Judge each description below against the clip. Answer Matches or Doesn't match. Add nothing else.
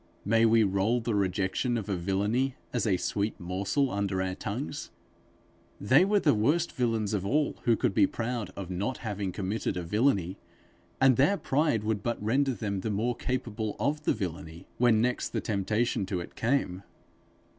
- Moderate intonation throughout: Matches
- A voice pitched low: Matches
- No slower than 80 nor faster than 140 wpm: Doesn't match